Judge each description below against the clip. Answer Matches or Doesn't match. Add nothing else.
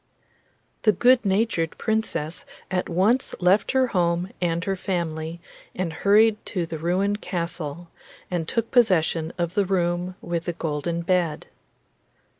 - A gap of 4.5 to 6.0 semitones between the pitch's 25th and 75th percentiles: Doesn't match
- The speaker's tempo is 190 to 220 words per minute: Doesn't match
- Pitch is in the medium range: Matches